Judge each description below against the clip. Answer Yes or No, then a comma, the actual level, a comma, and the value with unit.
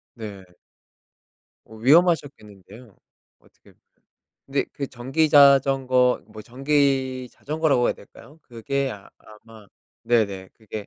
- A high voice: No, low, 125 Hz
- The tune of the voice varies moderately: Yes, average, 4.1 semitones